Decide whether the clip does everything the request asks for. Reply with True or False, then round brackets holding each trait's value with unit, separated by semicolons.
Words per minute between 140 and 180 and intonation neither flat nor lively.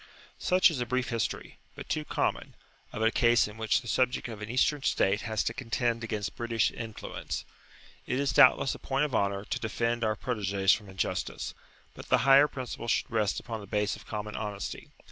False (200 wpm; 3.1 semitones)